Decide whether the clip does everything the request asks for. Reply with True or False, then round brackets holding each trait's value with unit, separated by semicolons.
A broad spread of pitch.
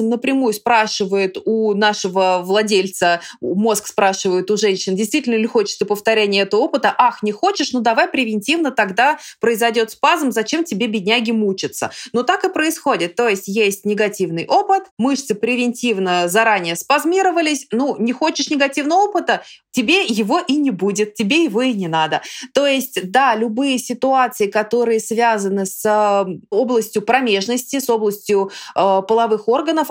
False (4.5 semitones)